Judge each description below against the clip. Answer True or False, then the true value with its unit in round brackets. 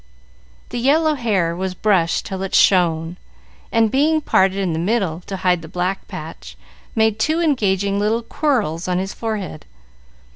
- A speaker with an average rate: True (155 wpm)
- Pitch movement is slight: False (4.3 semitones)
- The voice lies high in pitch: True (195 Hz)